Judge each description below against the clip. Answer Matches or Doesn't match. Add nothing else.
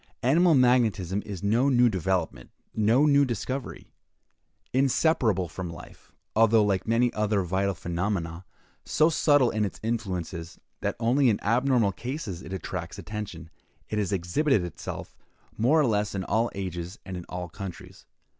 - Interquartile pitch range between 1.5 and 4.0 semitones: Doesn't match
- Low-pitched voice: Matches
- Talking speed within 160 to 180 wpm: Doesn't match